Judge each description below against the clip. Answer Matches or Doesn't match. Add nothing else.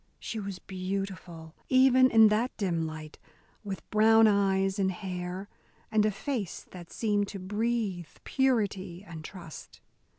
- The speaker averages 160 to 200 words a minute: Doesn't match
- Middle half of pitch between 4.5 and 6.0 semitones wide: Doesn't match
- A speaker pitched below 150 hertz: Doesn't match